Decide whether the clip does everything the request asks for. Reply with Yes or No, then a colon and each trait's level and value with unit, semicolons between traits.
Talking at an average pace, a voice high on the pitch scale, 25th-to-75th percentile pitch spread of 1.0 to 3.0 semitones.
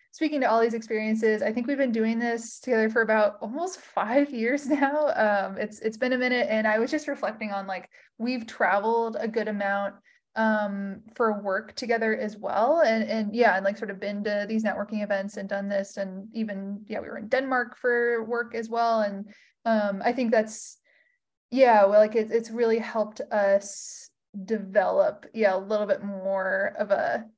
Yes: average, 195 wpm; high, 220 Hz; average, 2.7 semitones